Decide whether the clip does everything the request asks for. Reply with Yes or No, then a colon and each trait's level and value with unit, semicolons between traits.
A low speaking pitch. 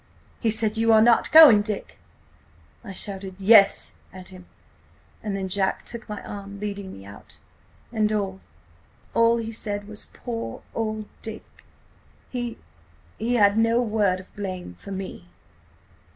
No: high, 205 Hz